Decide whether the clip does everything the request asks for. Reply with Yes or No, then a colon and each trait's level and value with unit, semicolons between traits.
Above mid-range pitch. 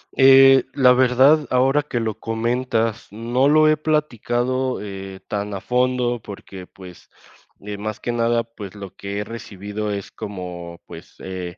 No: low, 115 Hz